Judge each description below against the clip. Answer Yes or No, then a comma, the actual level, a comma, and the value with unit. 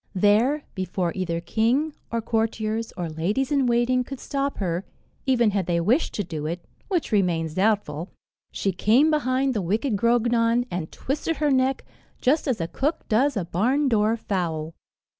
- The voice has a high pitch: Yes, high, 220 Hz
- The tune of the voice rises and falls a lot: Yes, wide, 6.2 semitones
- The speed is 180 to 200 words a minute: No, average, 165 wpm